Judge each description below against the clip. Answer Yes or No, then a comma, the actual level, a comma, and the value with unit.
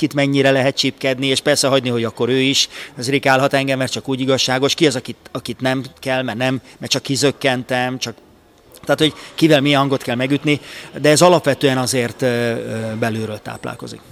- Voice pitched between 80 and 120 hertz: No, low, 130 Hz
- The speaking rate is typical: No, fast, 180 wpm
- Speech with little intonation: Yes, narrow, 2.0 semitones